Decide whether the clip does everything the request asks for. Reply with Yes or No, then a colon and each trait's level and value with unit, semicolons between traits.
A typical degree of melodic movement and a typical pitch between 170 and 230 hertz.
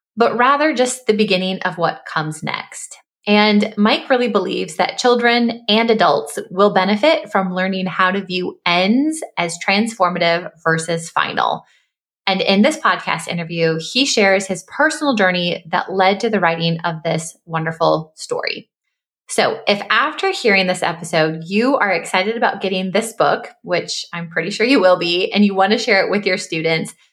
Yes: average, 4.7 semitones; high, 190 Hz